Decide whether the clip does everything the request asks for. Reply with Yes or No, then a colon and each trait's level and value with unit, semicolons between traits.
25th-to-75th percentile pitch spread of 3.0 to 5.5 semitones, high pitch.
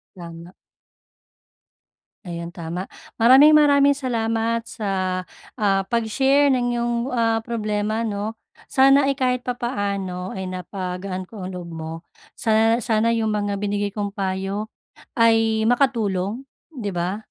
Yes: average, 3.8 semitones; high, 215 Hz